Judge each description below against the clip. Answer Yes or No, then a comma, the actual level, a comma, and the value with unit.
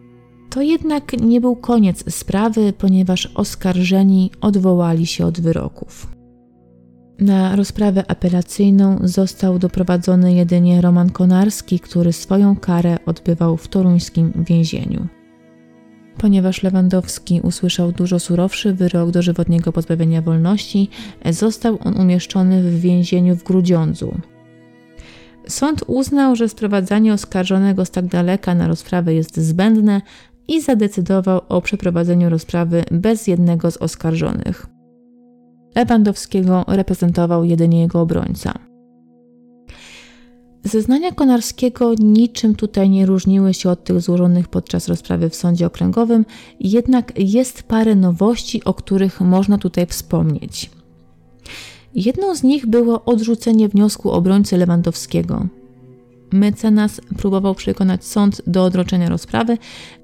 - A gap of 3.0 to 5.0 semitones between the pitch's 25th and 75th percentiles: Yes, average, 3.5 semitones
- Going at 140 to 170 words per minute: No, slow, 110 wpm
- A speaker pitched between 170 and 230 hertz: Yes, medium, 185 Hz